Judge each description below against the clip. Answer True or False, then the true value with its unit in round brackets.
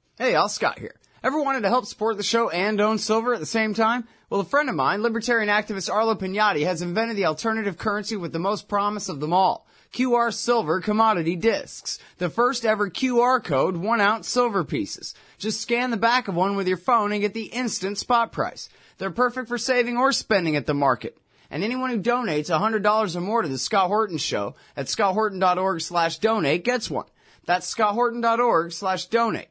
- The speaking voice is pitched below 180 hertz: False (215 Hz)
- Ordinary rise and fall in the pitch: True (3.7 semitones)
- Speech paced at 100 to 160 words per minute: False (200 wpm)